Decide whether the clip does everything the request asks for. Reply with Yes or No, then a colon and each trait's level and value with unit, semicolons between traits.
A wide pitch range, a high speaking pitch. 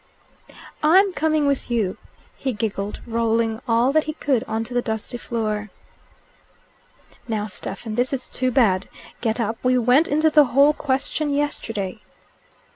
No: average, 4.2 semitones; high, 240 Hz